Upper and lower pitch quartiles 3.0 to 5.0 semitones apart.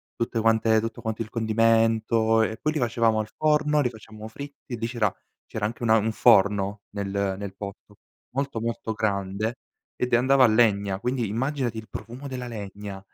No: narrow, 2.5 semitones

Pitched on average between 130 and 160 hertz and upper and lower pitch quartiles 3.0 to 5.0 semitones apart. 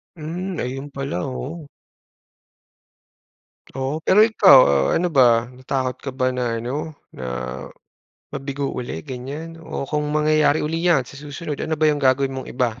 Yes: medium, 140 Hz; average, 3.3 semitones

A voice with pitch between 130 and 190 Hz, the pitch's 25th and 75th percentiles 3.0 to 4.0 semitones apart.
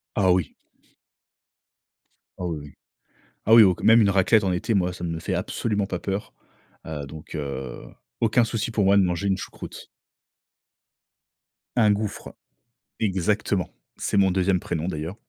No: very low, 95 Hz; average, 3.3 semitones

